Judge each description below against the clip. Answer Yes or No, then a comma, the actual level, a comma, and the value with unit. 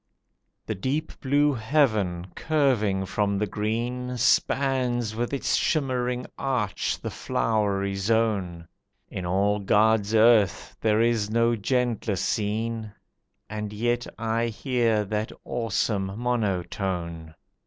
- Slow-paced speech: Yes, slow, 110 wpm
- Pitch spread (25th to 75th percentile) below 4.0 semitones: Yes, average, 3.3 semitones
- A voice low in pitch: Yes, low, 110 Hz